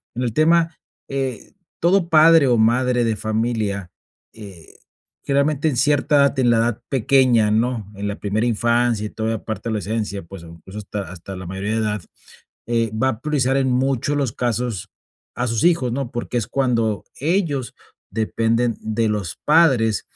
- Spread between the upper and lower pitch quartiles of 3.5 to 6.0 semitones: Yes, average, 3.9 semitones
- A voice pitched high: No, low, 115 Hz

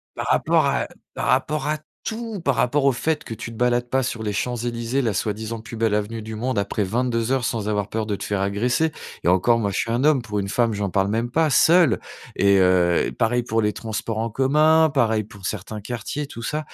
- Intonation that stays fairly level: No, average, 3.7 semitones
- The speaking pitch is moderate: No, low, 115 Hz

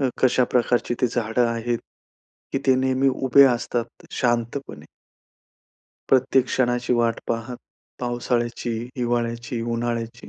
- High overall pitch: No, low, 120 Hz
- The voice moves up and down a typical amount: No, narrow, 1.4 semitones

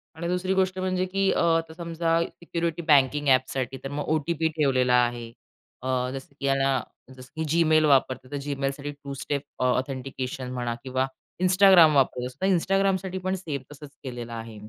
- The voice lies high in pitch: No, medium, 145 Hz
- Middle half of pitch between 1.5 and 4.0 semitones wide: No, average, 4.7 semitones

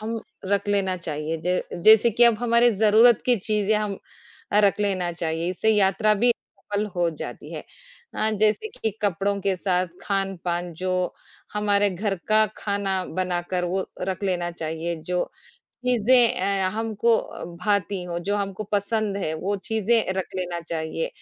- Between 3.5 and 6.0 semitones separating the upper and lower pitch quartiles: No, average, 3.1 semitones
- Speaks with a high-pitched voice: Yes, high, 200 Hz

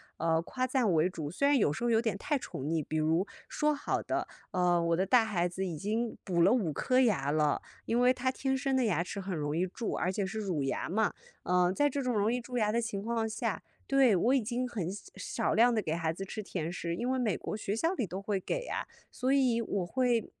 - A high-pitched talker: Yes, high, 210 Hz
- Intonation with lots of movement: Yes, wide, 5.8 semitones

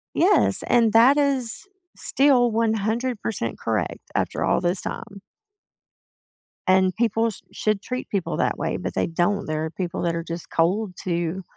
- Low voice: No, high, 205 Hz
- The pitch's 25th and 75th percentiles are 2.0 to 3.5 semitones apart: No, average, 5.0 semitones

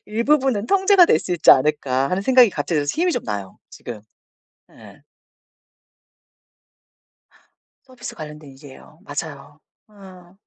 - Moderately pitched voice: Yes, medium, 175 Hz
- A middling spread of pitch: No, wide, 9.0 semitones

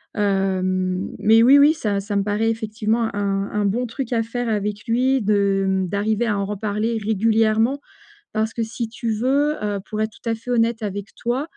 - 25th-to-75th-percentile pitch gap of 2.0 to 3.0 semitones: Yes, narrow, 2.4 semitones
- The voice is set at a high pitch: Yes, high, 220 Hz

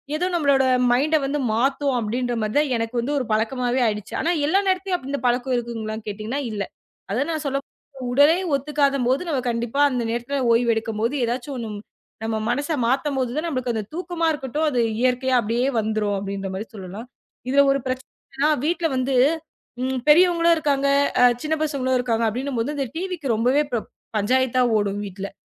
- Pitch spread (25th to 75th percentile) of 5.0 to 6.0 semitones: No, average, 3.8 semitones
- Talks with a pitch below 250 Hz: No, very high, 255 Hz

